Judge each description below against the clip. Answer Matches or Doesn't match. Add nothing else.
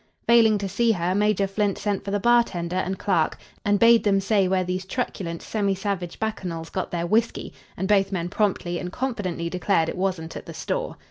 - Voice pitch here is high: Matches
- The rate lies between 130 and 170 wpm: Doesn't match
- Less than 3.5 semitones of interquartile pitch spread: Matches